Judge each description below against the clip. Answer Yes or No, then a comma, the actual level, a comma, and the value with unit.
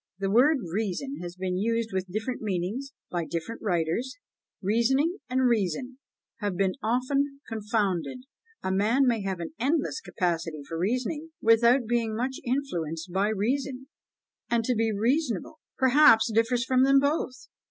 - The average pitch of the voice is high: Yes, high, 225 Hz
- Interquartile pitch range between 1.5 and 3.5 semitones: No, average, 5.3 semitones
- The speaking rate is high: No, average, 140 wpm